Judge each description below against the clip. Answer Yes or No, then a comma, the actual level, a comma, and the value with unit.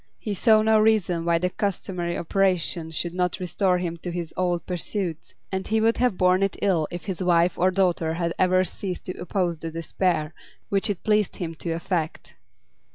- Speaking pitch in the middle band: Yes, medium, 180 Hz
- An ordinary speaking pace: Yes, average, 190 wpm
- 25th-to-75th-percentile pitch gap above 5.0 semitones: No, narrow, 2.4 semitones